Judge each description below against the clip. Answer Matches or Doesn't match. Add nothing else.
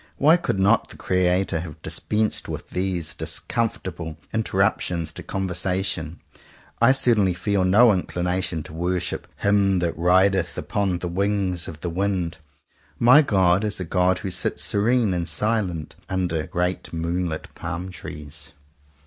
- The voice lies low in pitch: Matches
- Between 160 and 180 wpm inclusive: Doesn't match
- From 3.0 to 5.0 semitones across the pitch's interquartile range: Doesn't match